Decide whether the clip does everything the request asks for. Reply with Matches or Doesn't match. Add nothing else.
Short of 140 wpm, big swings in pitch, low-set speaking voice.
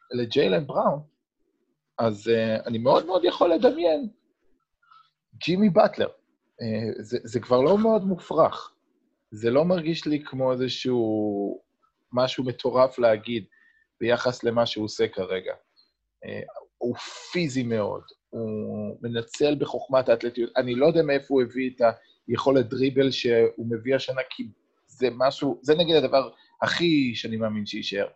Matches